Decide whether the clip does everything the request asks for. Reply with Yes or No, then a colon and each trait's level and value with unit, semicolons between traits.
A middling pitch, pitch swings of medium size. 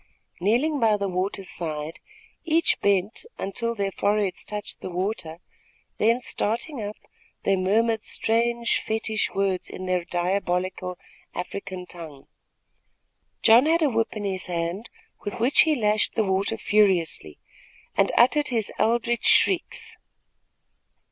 No: high, 205 Hz; average, 3.9 semitones